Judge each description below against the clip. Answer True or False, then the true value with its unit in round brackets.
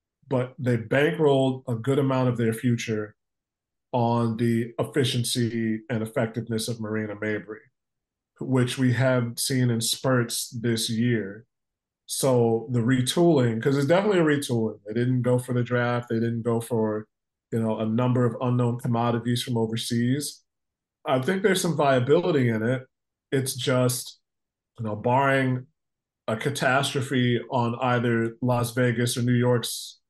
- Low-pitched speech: True (120 Hz)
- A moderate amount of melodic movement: False (2.1 semitones)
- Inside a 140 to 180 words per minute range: True (145 wpm)